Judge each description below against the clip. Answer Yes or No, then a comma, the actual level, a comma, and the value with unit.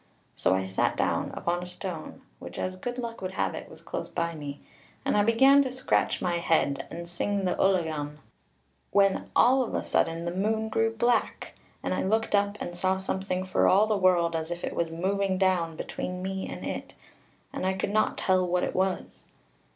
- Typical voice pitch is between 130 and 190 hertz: Yes, medium, 185 Hz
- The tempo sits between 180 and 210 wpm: Yes, fast, 205 wpm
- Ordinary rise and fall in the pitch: Yes, average, 3.0 semitones